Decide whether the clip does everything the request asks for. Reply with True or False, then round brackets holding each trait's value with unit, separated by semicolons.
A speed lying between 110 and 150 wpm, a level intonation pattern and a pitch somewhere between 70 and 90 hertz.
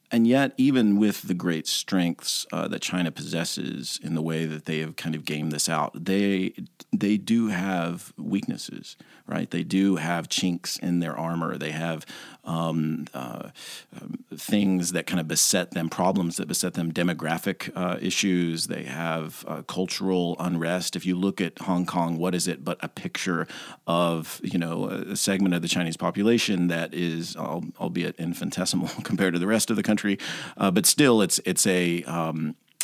False (175 wpm; 2.3 semitones; 85 Hz)